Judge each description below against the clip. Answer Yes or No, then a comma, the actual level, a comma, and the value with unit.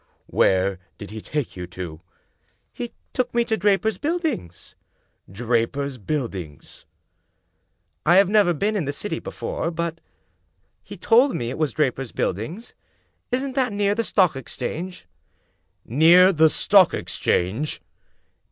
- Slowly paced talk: No, average, 145 wpm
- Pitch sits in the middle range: Yes, medium, 160 Hz